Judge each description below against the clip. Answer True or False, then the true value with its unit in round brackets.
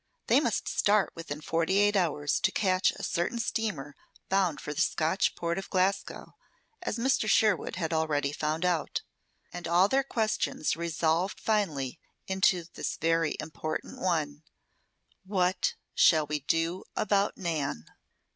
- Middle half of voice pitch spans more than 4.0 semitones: False (3.7 semitones)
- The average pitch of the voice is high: False (170 Hz)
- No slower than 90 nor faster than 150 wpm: True (140 wpm)